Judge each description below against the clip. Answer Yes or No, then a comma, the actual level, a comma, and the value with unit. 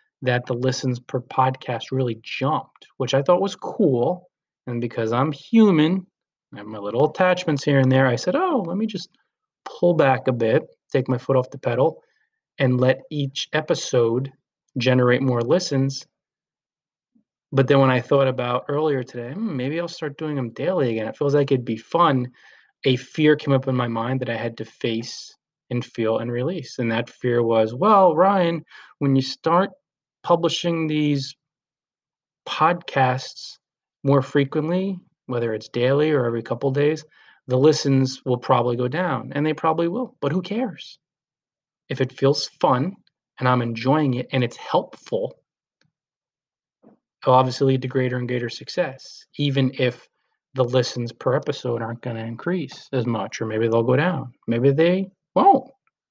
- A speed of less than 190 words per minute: Yes, average, 170 wpm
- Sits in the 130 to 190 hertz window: Yes, low, 135 Hz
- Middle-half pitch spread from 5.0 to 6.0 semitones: No, average, 4.4 semitones